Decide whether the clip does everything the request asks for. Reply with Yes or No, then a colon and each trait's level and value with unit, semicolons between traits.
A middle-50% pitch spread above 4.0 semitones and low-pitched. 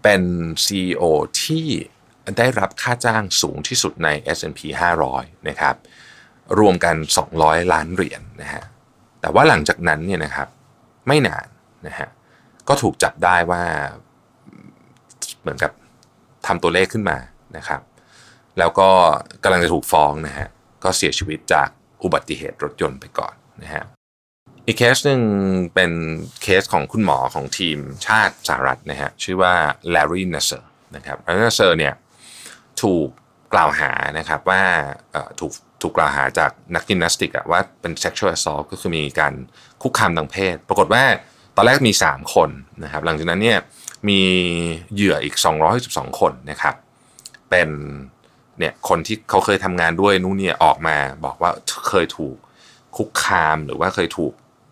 No: average, 3.6 semitones; very low, 90 Hz